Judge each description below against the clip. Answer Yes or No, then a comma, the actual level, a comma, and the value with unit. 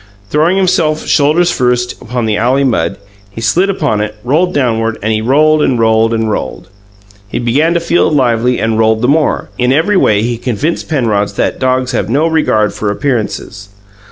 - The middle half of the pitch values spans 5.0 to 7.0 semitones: Yes, wide, 5.5 semitones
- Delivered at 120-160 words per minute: No, average, 180 wpm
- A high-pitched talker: No, low, 125 Hz